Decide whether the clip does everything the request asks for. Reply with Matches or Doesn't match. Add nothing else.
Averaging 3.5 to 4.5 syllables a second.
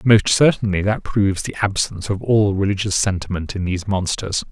Doesn't match